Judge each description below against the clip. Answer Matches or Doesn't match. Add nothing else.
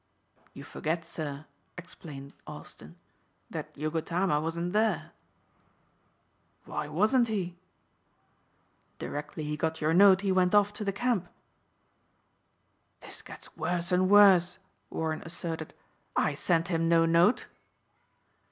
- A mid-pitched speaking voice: Matches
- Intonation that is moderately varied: Matches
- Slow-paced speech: Matches